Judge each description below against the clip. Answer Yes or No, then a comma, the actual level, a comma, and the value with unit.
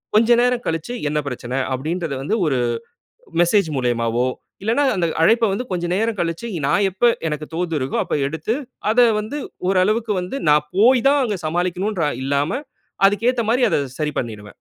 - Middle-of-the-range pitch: Yes, medium, 180 Hz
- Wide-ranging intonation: Yes, wide, 6.8 semitones